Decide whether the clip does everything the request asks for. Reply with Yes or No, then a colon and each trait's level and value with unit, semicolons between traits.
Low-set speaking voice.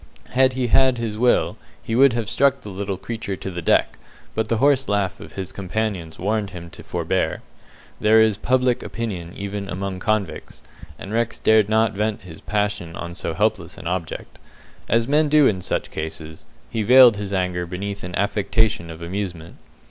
Yes: low, 105 Hz